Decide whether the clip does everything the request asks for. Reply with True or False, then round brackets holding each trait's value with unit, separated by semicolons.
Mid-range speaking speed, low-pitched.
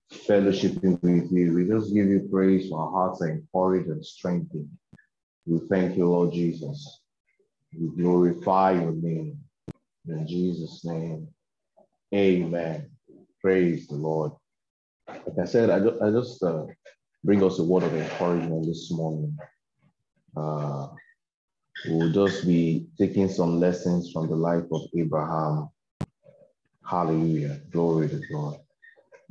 False (125 wpm; 85 Hz)